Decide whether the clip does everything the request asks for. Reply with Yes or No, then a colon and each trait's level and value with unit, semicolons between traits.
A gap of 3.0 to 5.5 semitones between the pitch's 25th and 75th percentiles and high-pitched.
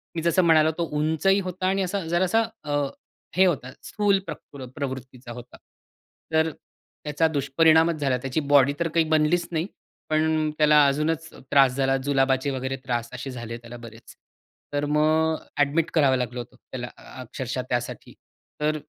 No: average, 3.7 semitones; medium, 150 Hz